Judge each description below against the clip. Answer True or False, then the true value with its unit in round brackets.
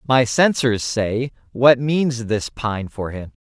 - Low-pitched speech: True (120 Hz)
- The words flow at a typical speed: True (160 wpm)